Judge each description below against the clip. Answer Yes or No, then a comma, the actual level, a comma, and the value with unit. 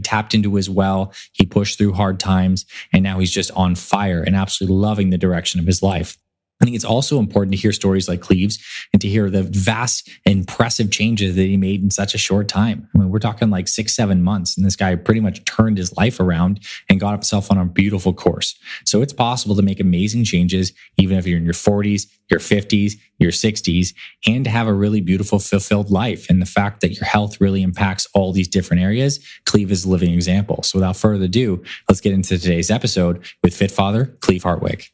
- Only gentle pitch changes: Yes, narrow, 2.0 semitones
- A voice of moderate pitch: No, low, 100 Hz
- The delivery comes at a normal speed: No, fast, 220 wpm